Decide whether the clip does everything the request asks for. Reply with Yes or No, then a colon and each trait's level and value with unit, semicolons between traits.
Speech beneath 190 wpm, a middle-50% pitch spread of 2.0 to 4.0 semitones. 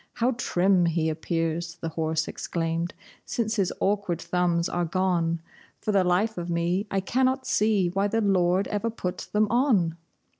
Yes: average, 160 wpm; average, 3.6 semitones